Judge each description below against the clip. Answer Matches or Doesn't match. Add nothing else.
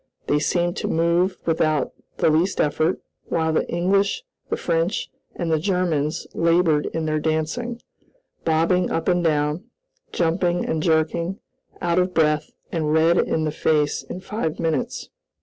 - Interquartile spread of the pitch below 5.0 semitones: Matches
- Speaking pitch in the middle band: Matches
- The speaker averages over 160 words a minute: Doesn't match